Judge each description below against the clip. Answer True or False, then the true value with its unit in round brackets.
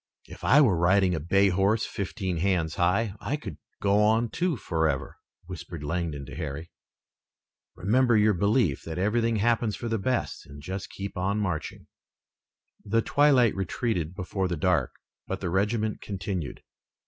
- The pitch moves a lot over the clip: False (4.2 semitones)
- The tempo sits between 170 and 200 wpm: False (155 wpm)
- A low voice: True (95 Hz)